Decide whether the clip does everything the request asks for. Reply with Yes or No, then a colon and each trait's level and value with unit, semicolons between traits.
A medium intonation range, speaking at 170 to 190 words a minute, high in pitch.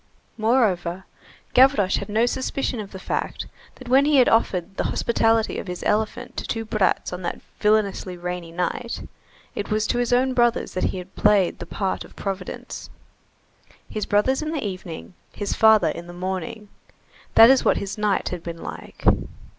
Yes: average, 4.2 semitones; average, 180 wpm; high, 210 Hz